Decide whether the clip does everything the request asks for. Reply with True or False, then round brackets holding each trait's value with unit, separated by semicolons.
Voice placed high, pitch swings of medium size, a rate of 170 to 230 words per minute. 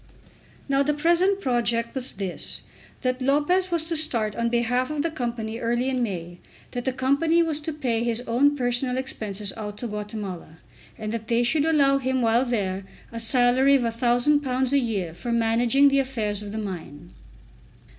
True (245 Hz; 3.7 semitones; 175 wpm)